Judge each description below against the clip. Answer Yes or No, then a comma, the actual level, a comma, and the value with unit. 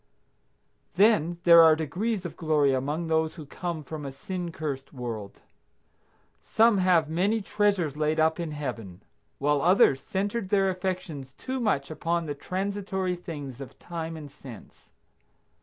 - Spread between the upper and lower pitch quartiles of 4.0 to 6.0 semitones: Yes, average, 4.4 semitones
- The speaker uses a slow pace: No, average, 145 wpm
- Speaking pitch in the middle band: Yes, medium, 160 Hz